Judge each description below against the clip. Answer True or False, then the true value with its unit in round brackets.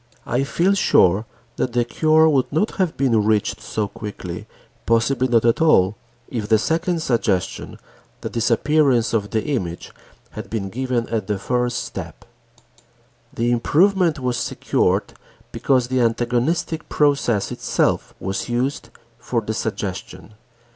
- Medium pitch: False (120 Hz)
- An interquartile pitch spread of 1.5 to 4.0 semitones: False (4.5 semitones)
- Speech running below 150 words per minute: True (135 wpm)